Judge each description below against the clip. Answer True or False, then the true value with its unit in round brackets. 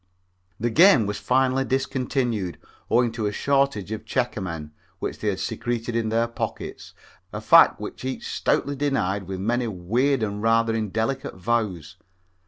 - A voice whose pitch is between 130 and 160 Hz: False (115 Hz)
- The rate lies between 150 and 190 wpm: True (155 wpm)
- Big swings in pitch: False (3.9 semitones)